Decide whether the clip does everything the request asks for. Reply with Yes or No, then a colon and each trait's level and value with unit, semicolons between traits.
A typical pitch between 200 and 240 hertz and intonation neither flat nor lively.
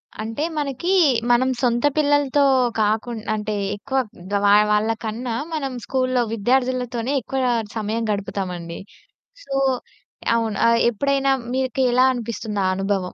Yes: high, 235 Hz; average, 3.7 semitones